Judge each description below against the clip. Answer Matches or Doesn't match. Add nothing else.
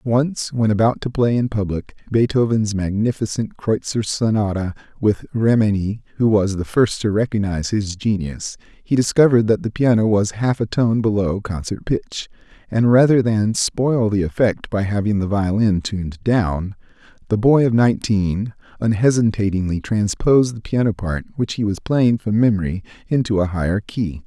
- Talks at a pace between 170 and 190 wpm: Doesn't match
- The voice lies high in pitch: Doesn't match